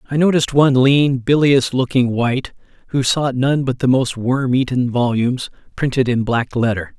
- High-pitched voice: No, low, 130 Hz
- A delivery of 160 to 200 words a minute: Yes, average, 170 wpm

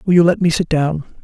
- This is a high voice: No, medium, 165 Hz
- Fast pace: Yes, fast, 290 wpm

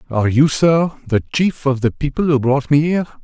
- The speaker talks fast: Yes, fast, 225 wpm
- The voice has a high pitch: No, medium, 140 Hz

